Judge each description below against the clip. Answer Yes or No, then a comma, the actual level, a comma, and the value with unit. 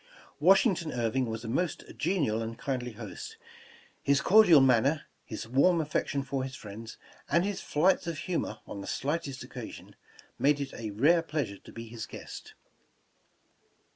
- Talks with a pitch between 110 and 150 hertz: Yes, medium, 140 Hz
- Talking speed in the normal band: Yes, average, 160 wpm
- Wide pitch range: Yes, wide, 6.3 semitones